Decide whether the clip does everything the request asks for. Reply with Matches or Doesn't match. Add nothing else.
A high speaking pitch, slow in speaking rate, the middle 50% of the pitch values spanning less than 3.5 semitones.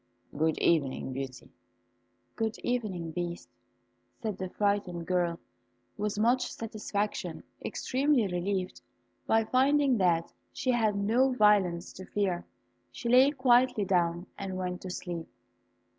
Doesn't match